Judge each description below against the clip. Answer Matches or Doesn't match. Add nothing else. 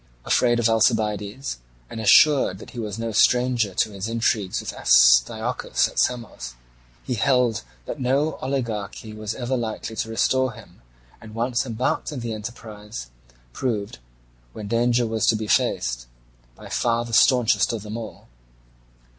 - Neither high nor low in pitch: Doesn't match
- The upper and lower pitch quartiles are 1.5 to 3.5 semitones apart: Matches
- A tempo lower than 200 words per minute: Matches